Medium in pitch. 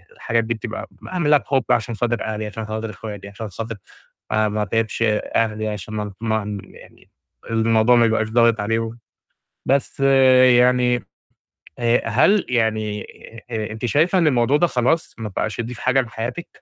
No: low, 115 Hz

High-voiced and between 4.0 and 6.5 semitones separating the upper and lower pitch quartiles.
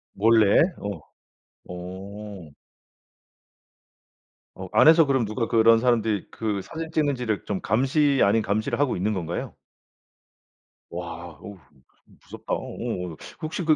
No: low, 110 Hz; average, 5.3 semitones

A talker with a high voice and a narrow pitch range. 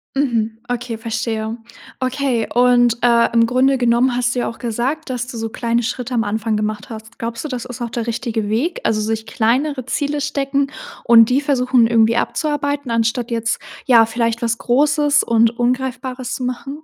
Yes: high, 240 Hz; narrow, 2.3 semitones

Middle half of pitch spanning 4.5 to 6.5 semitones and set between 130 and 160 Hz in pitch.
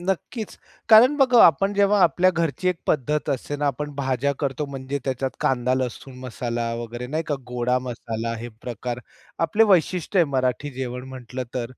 Yes: average, 5.2 semitones; low, 135 Hz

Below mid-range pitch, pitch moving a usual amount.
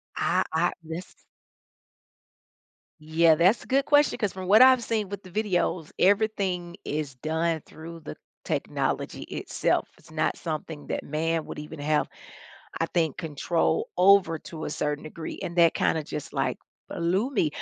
No: medium, 170 Hz; average, 3.6 semitones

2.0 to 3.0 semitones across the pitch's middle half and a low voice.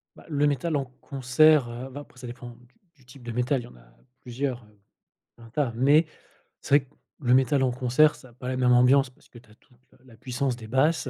Yes: narrow, 2.5 semitones; low, 130 Hz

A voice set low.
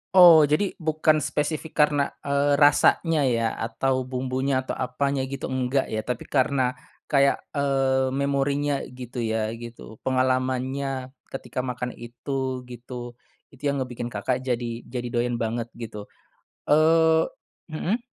Yes: low, 130 Hz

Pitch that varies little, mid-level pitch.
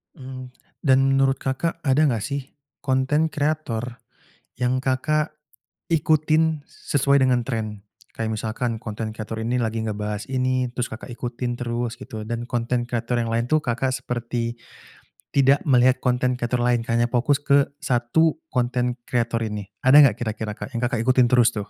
No: narrow, 2.3 semitones; low, 125 Hz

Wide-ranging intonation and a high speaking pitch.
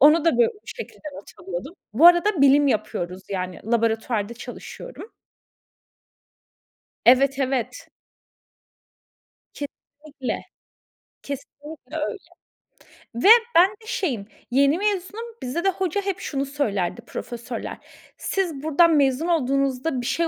Yes: wide, 5.7 semitones; very high, 280 Hz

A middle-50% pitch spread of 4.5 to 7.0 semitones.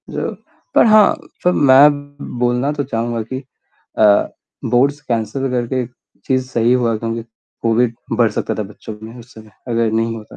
No: narrow, 2.5 semitones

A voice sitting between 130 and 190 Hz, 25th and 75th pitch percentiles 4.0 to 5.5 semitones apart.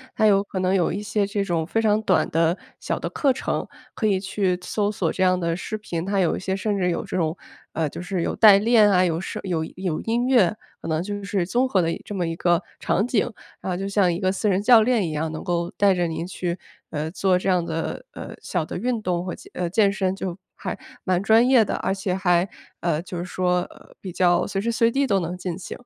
No: medium, 185 Hz; average, 2.9 semitones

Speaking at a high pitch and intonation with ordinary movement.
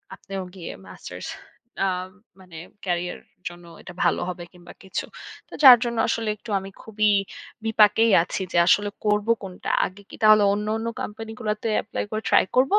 Yes: high, 210 Hz; average, 3.2 semitones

